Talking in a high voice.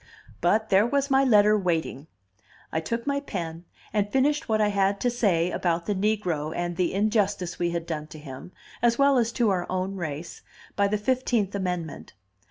Yes: high, 200 Hz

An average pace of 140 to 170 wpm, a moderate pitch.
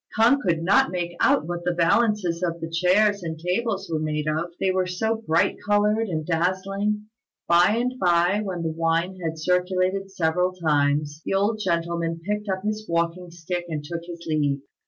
No: average, 185 wpm; medium, 175 Hz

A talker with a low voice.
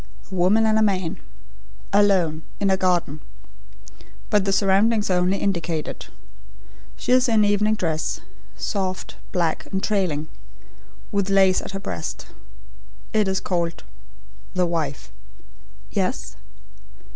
No: high, 190 Hz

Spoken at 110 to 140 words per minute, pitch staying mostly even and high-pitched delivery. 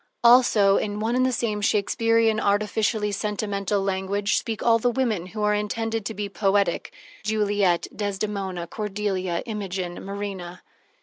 Yes: slow, 135 wpm; narrow, 1.9 semitones; high, 205 Hz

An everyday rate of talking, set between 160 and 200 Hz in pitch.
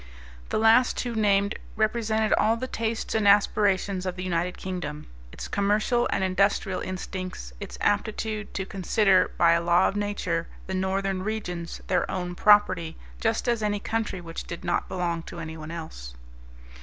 Yes: average, 160 wpm; high, 190 Hz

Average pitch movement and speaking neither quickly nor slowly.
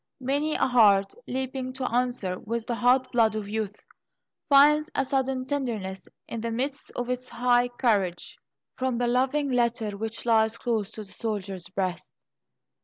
Yes: average, 3.2 semitones; average, 160 wpm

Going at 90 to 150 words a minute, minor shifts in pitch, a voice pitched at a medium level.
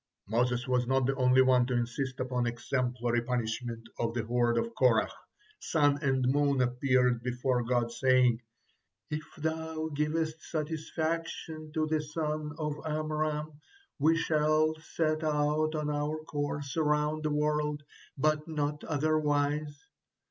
No: slow, 135 wpm; average, 3.5 semitones; medium, 145 Hz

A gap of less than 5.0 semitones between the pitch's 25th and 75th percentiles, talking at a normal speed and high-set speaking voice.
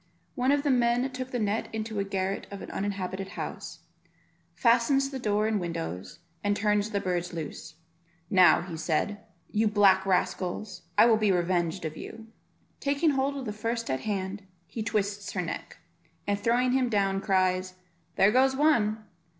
Yes: average, 3.9 semitones; average, 170 wpm; high, 205 Hz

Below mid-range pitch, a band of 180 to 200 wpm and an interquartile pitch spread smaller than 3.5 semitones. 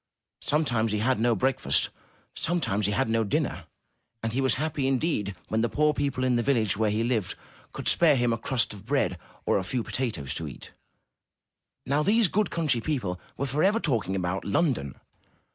No: low, 120 Hz; average, 190 wpm; average, 5.2 semitones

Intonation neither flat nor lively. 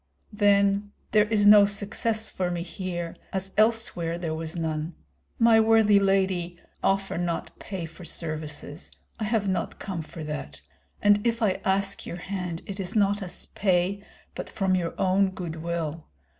Yes: average, 3.2 semitones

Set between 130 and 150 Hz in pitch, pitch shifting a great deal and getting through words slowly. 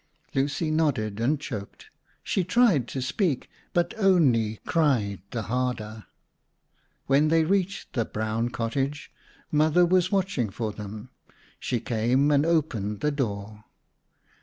Yes: low, 135 Hz; wide, 6.3 semitones; slow, 125 wpm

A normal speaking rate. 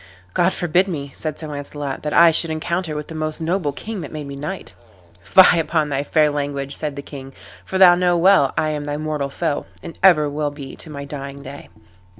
No: fast, 215 wpm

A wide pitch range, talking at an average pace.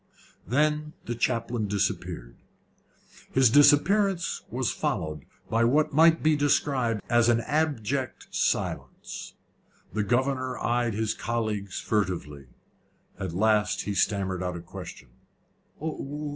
No: wide, 5.7 semitones; slow, 110 wpm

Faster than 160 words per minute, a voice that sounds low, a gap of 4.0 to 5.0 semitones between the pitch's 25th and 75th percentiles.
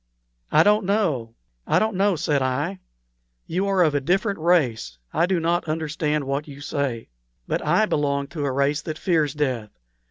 No: average, 180 wpm; medium, 150 Hz; average, 4.3 semitones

